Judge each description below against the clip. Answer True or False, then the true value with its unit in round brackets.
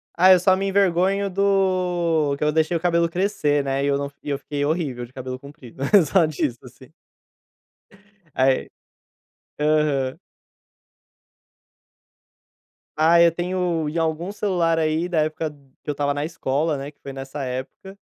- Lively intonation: False (3.9 semitones)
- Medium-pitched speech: True (155 Hz)